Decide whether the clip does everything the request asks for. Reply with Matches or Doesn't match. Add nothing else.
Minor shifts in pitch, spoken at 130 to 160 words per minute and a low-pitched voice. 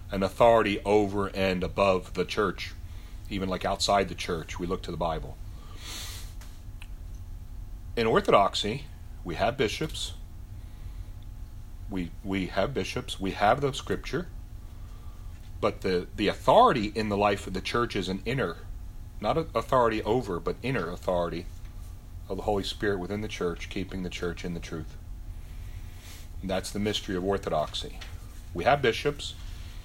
Matches